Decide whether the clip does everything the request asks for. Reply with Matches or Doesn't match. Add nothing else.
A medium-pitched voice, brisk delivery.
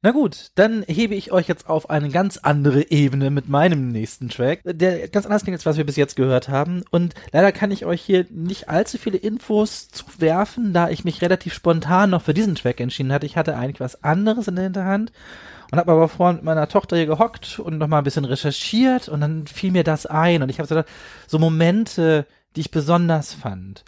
Matches